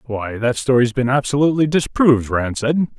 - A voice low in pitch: Yes, low, 130 Hz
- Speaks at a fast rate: No, average, 160 wpm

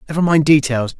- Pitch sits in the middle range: Yes, medium, 145 Hz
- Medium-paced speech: Yes, average, 180 wpm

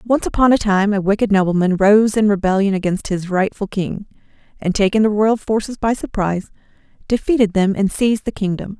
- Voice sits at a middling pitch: No, high, 205 Hz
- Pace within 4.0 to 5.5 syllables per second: No, 5.7 syllables/s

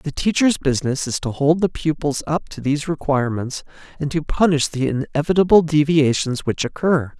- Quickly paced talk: No, average, 165 wpm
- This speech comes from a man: Yes, male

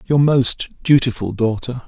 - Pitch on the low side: Yes, low, 125 Hz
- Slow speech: Yes, slow, 130 wpm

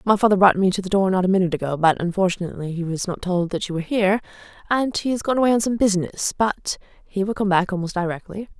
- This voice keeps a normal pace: No, fast, 250 wpm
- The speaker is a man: No, female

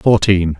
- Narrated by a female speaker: No, male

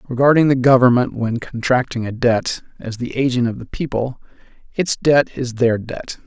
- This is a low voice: Yes, low, 125 Hz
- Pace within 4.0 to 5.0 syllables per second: Yes, 4.8 syllables/s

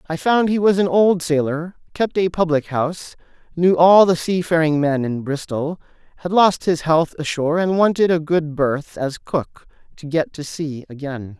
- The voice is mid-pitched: Yes, medium, 160 Hz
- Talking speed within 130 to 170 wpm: No, average, 185 wpm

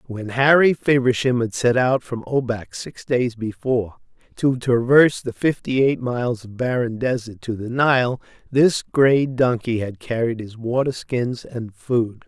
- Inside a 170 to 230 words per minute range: No, average, 160 wpm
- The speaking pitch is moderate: No, low, 125 Hz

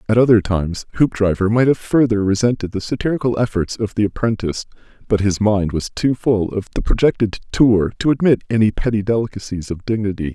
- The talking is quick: No, average, 180 wpm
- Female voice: No, male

